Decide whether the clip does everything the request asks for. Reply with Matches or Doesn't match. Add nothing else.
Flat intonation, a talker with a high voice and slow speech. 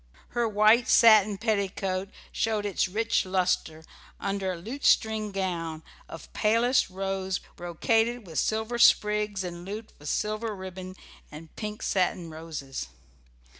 Doesn't match